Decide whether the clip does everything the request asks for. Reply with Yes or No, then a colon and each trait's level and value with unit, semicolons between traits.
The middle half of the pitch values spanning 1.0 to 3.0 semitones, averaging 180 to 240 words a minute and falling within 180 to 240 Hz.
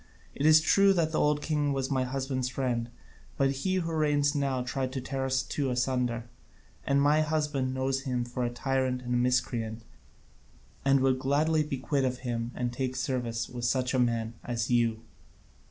No: narrow, 2.5 semitones; average, 185 wpm; low, 130 Hz